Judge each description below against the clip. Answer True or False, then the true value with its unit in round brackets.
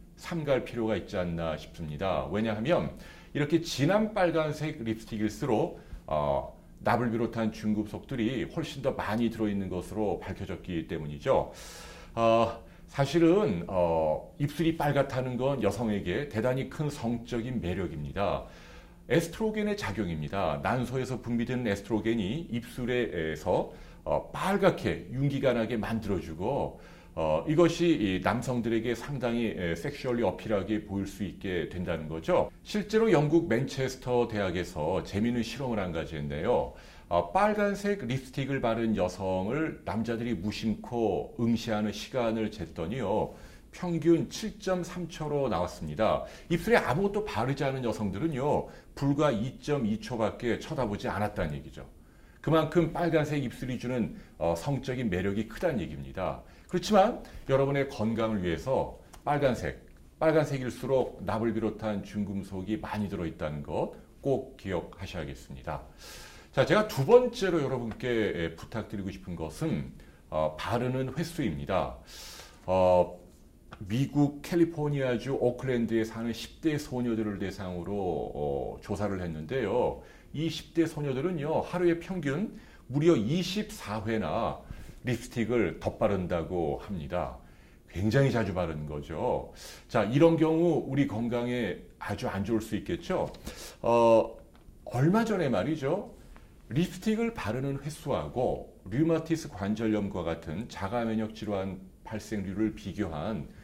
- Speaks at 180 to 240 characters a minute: False (290 characters per minute)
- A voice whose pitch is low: True (115 Hz)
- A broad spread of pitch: True (6.4 semitones)